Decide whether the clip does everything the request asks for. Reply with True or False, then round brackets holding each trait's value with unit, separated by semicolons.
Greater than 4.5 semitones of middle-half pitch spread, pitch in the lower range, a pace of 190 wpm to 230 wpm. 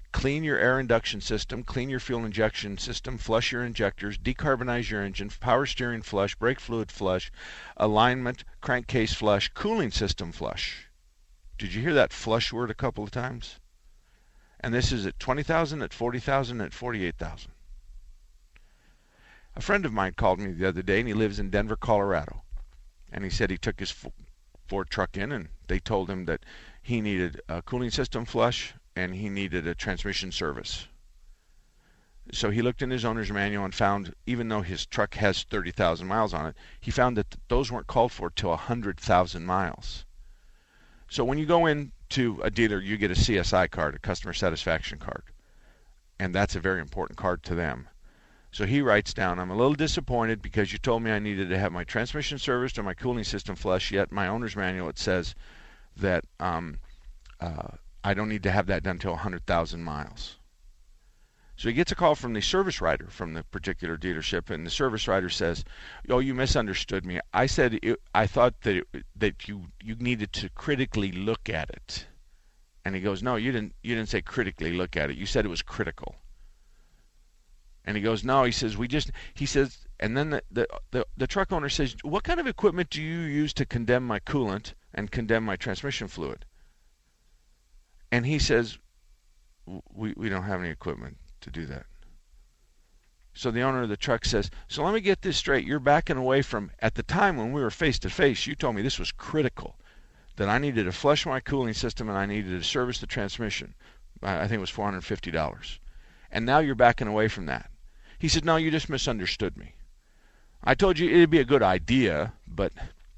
True (5.0 semitones; 105 Hz; 195 wpm)